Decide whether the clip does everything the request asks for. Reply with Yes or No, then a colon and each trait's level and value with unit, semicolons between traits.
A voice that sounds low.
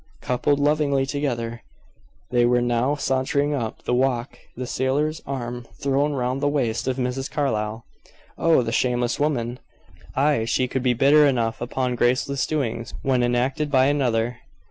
Yes: low, 130 Hz